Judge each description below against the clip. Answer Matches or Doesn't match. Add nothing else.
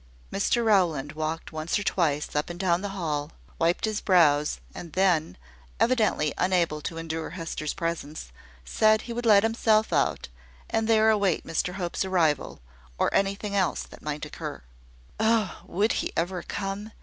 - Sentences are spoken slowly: Doesn't match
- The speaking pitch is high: Doesn't match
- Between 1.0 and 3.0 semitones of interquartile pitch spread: Doesn't match